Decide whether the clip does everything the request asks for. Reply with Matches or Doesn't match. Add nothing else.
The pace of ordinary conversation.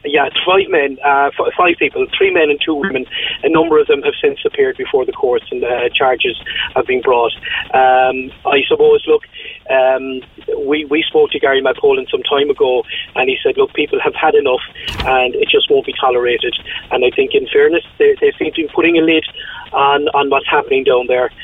Doesn't match